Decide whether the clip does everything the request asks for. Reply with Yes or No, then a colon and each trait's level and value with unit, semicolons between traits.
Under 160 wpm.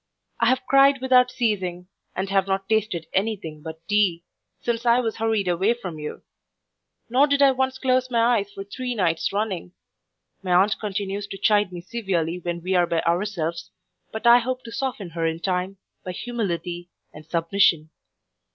No: average, 180 wpm